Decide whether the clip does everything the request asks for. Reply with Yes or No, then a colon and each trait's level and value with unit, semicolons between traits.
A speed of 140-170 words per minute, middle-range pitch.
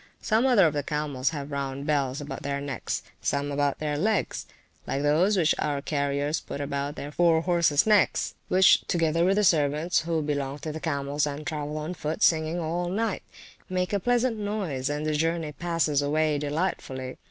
No: average, 185 wpm; medium, 155 Hz